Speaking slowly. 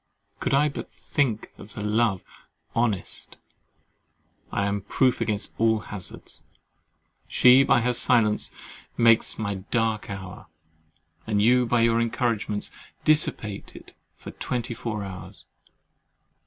Yes: slow, 115 wpm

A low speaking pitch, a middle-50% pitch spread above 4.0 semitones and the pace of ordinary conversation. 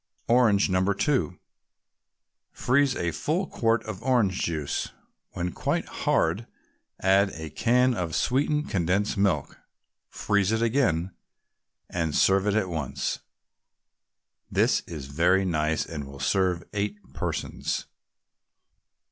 No: very low, 95 Hz; average, 5.2 semitones; slow, 115 wpm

